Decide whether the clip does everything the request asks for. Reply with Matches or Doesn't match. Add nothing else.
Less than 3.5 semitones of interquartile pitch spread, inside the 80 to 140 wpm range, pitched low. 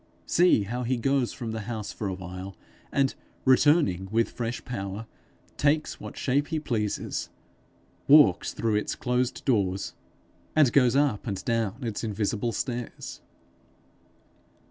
Doesn't match